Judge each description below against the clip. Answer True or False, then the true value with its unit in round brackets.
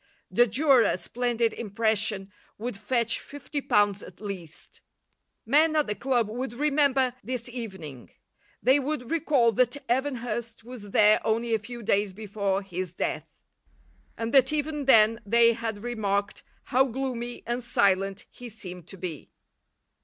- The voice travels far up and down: False (3.7 semitones)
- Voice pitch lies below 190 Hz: False (230 Hz)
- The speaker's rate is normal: True (145 wpm)